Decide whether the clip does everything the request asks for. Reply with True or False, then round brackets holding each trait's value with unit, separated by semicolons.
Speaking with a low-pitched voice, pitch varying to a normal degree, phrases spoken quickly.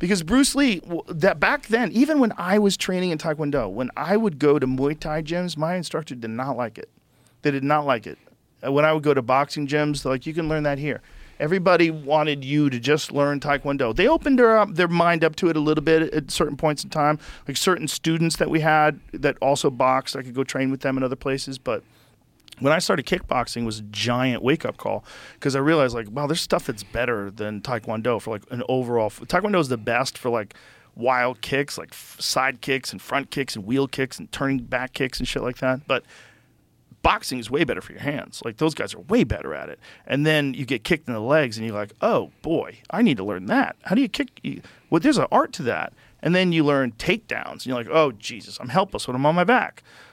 False (145 Hz; 3.9 semitones; 245 wpm)